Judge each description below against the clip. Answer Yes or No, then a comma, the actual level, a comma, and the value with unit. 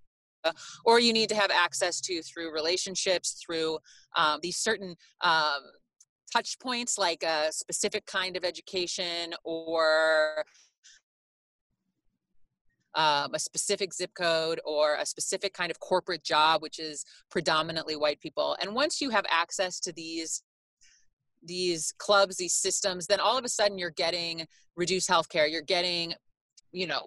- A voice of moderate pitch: Yes, medium, 175 Hz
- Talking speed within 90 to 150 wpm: Yes, average, 145 wpm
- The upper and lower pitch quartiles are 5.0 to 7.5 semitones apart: No, average, 3.1 semitones